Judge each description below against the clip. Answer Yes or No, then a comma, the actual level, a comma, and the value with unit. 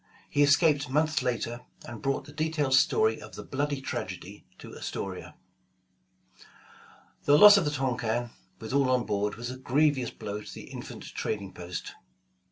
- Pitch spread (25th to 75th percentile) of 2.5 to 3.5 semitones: No, average, 4.9 semitones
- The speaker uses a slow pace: No, average, 160 wpm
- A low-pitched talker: Yes, low, 130 Hz